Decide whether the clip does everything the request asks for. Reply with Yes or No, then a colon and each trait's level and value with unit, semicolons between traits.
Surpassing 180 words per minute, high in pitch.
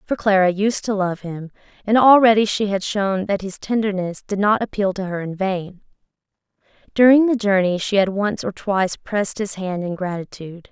Yes: average, 190 wpm; high, 200 Hz